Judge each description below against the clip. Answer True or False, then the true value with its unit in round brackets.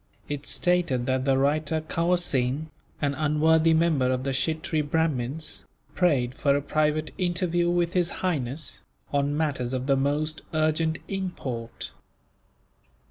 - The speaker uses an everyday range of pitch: True (3.2 semitones)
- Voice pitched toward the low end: False (155 Hz)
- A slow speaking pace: True (130 wpm)